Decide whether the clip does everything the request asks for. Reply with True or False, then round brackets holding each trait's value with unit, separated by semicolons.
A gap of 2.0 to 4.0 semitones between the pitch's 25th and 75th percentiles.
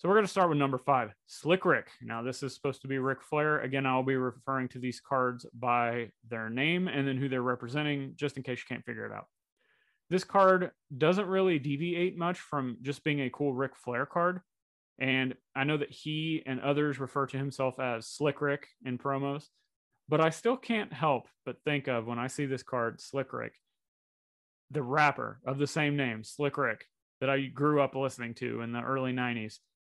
True (2.7 semitones)